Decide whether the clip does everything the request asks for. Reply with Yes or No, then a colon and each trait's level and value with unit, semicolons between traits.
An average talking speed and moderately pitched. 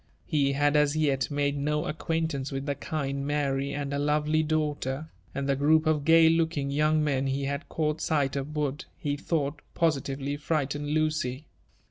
Yes: average, 170 wpm; medium, 145 Hz